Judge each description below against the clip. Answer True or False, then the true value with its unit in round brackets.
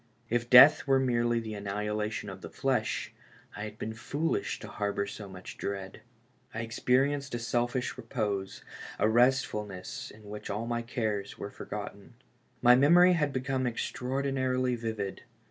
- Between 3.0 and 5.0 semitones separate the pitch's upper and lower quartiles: True (3.6 semitones)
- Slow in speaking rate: False (145 wpm)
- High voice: False (120 Hz)